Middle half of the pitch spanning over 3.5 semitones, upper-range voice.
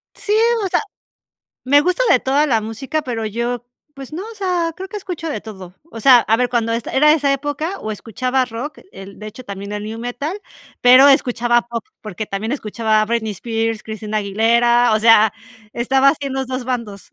Yes: average, 4.0 semitones; high, 240 Hz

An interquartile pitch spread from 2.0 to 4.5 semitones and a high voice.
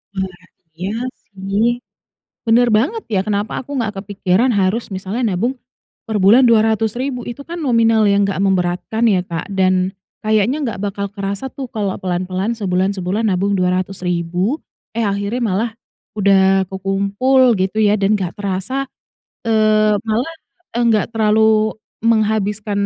Yes: average, 2.8 semitones; high, 205 Hz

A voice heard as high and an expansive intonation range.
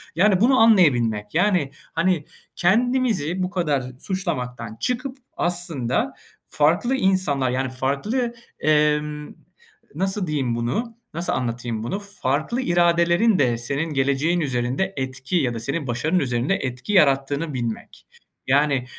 No: medium, 150 Hz; wide, 6.3 semitones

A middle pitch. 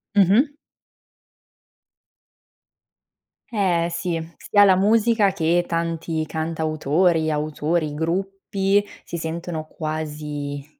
Yes: medium, 165 Hz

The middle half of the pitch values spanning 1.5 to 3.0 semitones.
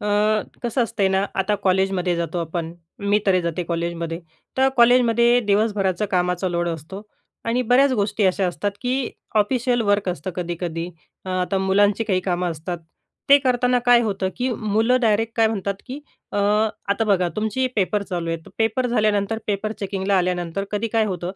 No: average, 3.8 semitones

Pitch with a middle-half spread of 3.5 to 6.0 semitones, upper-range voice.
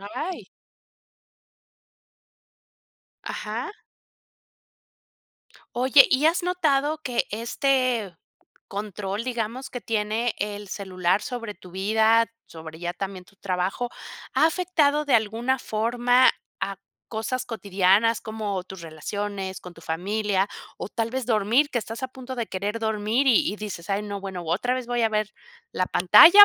Yes: average, 4.2 semitones; high, 220 Hz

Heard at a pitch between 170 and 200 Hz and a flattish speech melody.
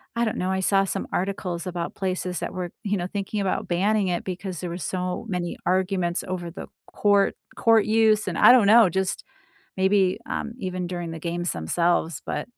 Yes: medium, 185 Hz; narrow, 2.3 semitones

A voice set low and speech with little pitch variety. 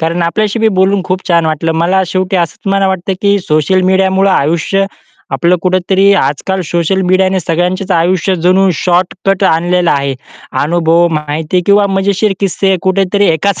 No: medium, 185 Hz; narrow, 2.3 semitones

